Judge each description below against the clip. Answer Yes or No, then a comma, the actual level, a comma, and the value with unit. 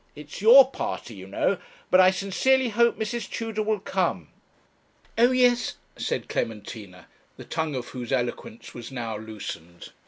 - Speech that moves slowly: No, average, 150 wpm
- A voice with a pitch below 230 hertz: Yes, medium, 185 Hz